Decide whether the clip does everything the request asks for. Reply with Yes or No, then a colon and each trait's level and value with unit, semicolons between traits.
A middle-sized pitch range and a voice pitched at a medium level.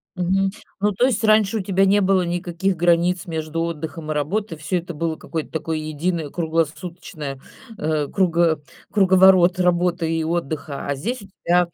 Yes: average, 3.0 semitones; medium, 175 Hz